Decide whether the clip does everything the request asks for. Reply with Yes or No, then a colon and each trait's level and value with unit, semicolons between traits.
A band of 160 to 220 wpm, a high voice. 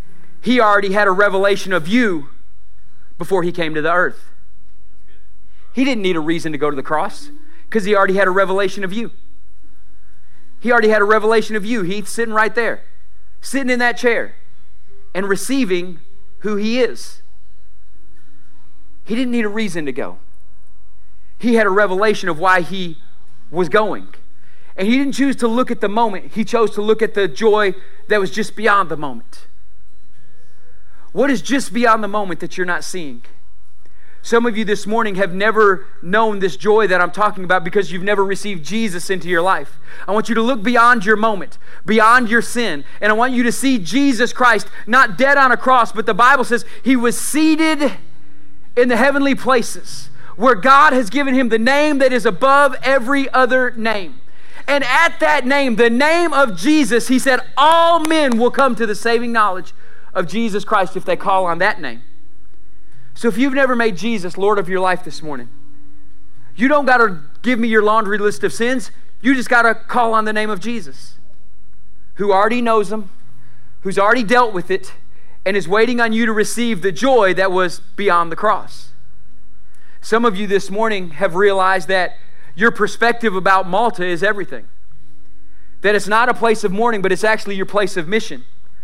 Yes: average, 190 wpm; high, 205 Hz